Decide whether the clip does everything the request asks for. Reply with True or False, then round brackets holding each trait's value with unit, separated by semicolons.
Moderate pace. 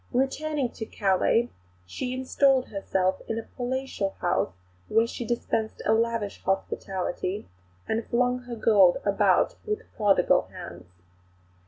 False (125 wpm)